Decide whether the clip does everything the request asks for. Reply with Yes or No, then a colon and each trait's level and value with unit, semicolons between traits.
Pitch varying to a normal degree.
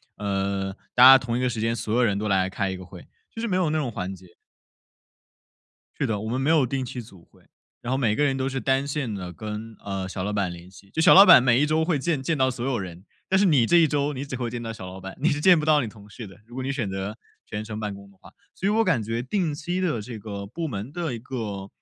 No: wide, 6.0 semitones